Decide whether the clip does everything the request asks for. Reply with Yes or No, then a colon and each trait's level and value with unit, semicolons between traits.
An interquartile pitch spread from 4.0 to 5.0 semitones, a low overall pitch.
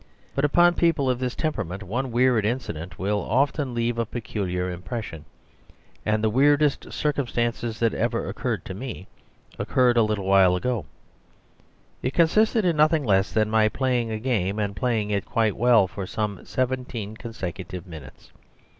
Yes: average, 4.4 semitones; low, 115 Hz